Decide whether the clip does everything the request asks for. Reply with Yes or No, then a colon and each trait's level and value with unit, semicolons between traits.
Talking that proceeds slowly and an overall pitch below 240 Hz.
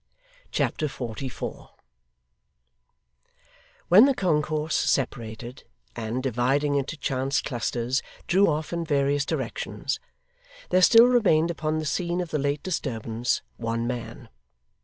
Yes: slow, 115 wpm; medium, 140 Hz